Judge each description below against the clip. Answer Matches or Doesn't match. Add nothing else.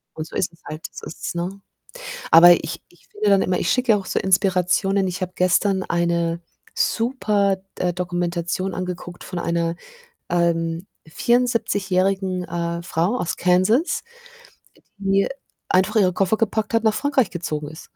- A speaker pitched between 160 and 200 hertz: Matches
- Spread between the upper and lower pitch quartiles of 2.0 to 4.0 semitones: Matches